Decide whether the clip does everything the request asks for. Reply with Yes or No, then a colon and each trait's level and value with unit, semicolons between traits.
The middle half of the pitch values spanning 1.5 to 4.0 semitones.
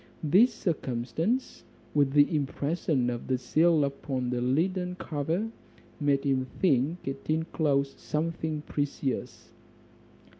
Yes: average, 3.6 semitones